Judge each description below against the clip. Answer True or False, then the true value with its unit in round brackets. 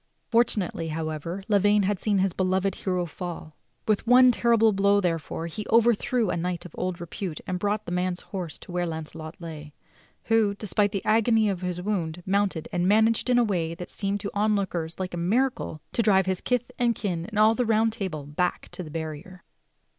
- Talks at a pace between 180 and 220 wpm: True (200 wpm)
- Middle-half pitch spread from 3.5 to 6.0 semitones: True (3.8 semitones)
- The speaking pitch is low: False (190 Hz)